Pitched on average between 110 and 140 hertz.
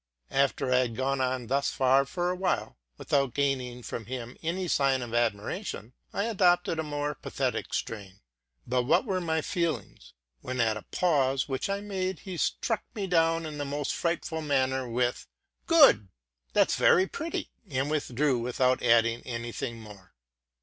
Yes: low, 135 Hz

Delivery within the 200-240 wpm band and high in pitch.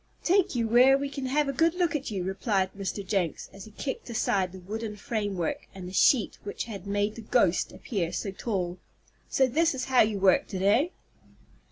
Yes: fast, 205 wpm; high, 215 Hz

